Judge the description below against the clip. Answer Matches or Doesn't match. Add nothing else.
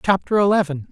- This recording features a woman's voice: Doesn't match